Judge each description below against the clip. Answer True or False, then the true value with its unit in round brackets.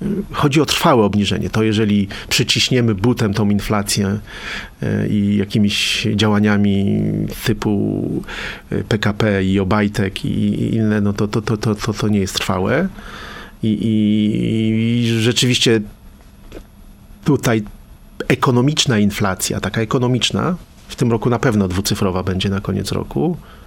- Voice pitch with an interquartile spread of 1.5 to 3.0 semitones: True (2.4 semitones)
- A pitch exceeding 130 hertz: False (105 Hz)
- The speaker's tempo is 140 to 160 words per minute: False (120 wpm)